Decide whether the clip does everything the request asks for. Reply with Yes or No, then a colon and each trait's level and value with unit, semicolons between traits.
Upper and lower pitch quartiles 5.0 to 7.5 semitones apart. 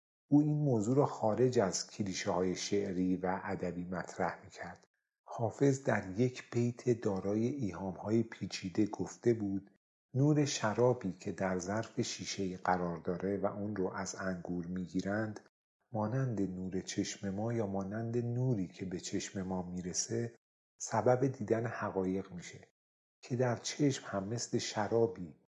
No: average, 4.1 semitones